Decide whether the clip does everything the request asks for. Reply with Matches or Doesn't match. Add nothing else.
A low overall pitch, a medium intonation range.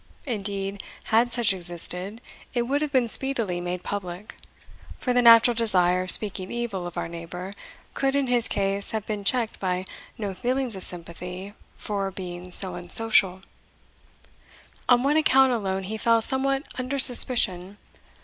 Doesn't match